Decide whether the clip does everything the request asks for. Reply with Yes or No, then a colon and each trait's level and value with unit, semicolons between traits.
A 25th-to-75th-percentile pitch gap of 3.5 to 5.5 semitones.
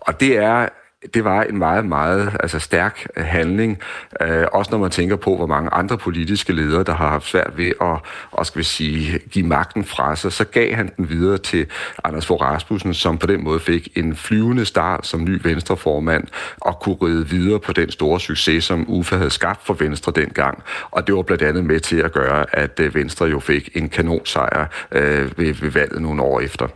No: average, 3.1 semitones